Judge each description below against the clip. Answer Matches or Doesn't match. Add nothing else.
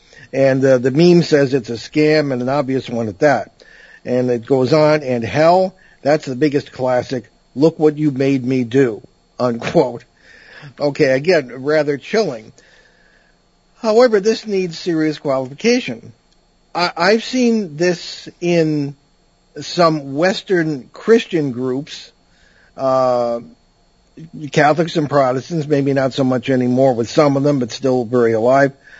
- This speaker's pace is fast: Doesn't match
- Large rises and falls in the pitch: Doesn't match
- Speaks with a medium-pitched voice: Matches